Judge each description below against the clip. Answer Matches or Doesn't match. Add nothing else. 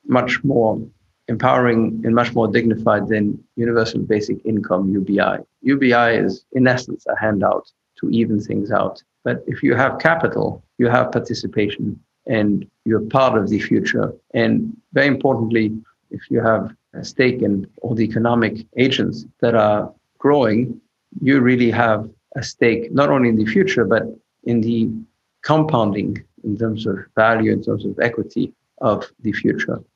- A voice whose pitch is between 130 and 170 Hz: Doesn't match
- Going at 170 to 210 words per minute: Doesn't match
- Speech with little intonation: Matches